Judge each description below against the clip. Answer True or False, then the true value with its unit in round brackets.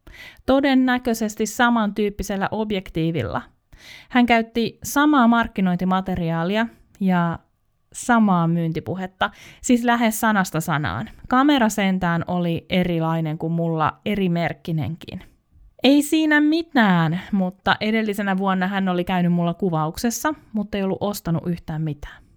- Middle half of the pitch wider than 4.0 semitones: True (5.3 semitones)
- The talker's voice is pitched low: False (190 Hz)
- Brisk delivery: False (105 wpm)